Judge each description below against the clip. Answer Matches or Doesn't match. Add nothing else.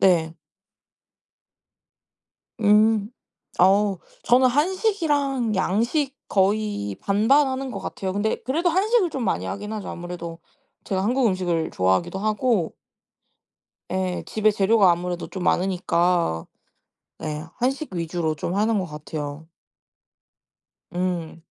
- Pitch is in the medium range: Doesn't match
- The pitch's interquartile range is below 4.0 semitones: Doesn't match